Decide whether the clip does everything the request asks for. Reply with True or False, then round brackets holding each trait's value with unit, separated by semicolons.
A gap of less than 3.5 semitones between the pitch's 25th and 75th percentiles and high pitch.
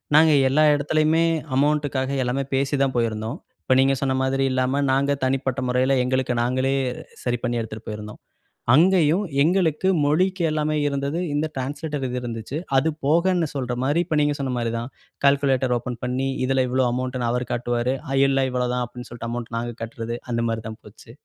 False (3.0 semitones; 130 Hz)